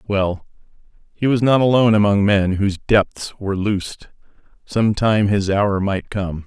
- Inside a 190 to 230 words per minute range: No, average, 160 wpm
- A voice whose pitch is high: No, low, 100 Hz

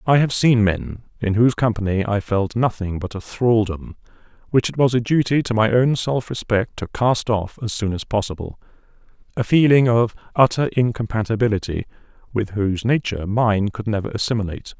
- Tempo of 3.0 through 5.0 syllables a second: No, 5.4 syllables/s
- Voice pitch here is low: Yes, low, 110 Hz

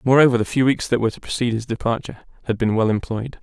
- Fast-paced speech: Yes, fast, 245 wpm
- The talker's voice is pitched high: No, low, 120 Hz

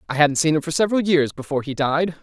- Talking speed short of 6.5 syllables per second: No, 6.9 syllables/s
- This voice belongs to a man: Yes, male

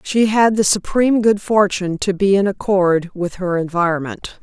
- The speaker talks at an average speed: Yes, average, 175 wpm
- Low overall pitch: No, high, 195 Hz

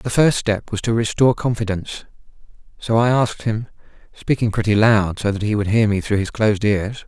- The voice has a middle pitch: No, low, 110 Hz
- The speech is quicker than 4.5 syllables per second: Yes, 5.6 syllables/s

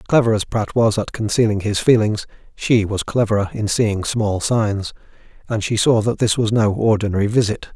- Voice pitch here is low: Yes, low, 110 Hz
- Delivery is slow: No, average, 185 wpm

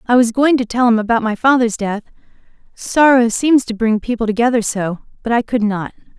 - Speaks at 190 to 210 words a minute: Yes, fast, 205 wpm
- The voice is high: Yes, high, 230 Hz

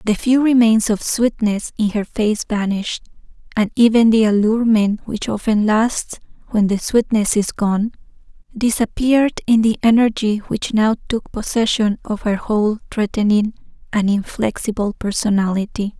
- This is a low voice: No, high, 215 Hz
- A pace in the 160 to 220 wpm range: No, slow, 135 wpm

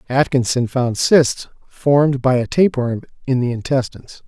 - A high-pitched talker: No, low, 130 Hz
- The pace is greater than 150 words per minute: No, average, 140 wpm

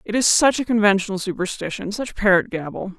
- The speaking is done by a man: No, female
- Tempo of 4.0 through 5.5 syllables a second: No, 5.9 syllables/s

